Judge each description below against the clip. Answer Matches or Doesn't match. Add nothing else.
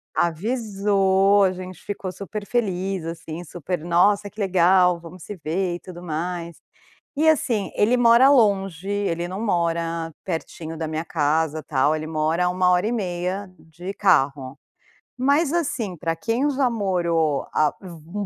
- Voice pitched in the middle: Matches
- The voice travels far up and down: Doesn't match